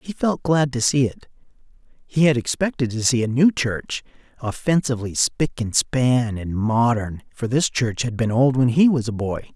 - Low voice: Yes, low, 125 Hz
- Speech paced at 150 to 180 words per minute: No, average, 195 wpm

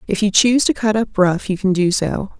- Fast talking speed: Yes, fast, 275 wpm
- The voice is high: Yes, high, 205 Hz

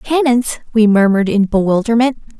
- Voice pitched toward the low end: No, high, 225 Hz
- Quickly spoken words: No, slow, 125 wpm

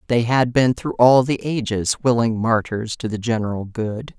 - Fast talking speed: No, average, 185 wpm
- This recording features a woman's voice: Yes, female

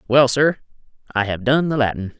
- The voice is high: No, low, 125 Hz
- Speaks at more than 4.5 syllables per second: Yes, 5.4 syllables/s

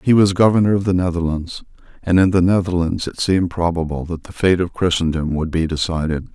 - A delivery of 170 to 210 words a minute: Yes, average, 200 wpm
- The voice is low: Yes, very low, 90 Hz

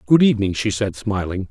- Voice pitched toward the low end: Yes, low, 105 Hz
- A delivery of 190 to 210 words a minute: Yes, average, 200 wpm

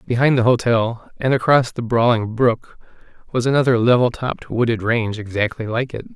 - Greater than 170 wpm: No, average, 165 wpm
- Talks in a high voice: No, low, 120 Hz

